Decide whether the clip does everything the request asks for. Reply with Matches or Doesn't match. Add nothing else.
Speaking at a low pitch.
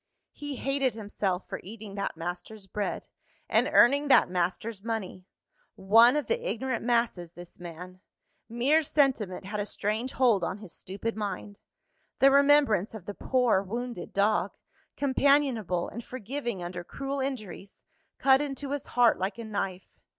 Doesn't match